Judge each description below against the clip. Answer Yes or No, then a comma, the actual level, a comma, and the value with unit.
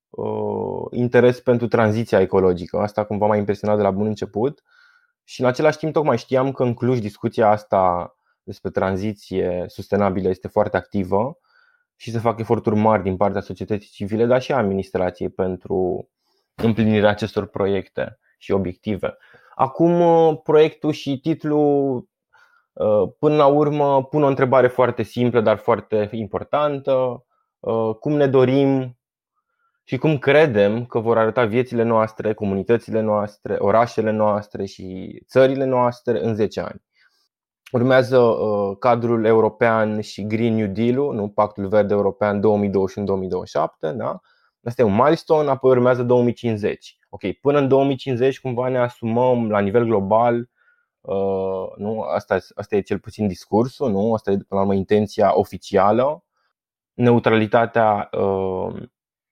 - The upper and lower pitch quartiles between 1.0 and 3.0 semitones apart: No, average, 4.3 semitones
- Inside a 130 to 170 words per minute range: Yes, average, 135 wpm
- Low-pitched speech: Yes, low, 115 Hz